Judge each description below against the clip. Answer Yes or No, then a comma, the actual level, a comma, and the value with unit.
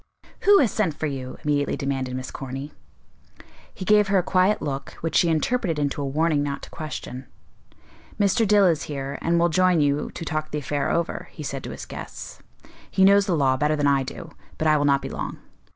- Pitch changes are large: No, average, 4.5 semitones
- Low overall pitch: No, medium, 155 Hz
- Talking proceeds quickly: Yes, fast, 215 wpm